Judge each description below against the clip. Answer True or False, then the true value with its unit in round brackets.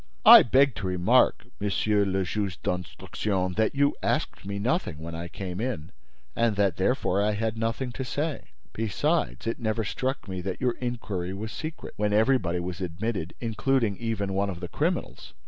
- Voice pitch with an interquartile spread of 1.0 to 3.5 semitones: False (4.1 semitones)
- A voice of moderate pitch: False (105 Hz)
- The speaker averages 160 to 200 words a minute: True (170 wpm)